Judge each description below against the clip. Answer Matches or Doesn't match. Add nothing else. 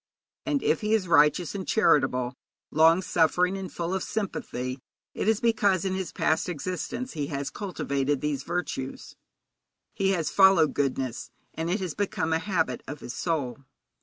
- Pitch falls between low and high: Matches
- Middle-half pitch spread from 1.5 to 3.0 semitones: Doesn't match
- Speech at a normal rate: Matches